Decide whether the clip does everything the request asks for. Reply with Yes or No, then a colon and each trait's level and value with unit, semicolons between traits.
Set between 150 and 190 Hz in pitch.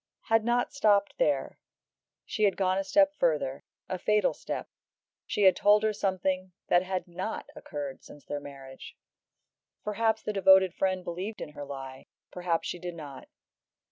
Yes: medium, 185 Hz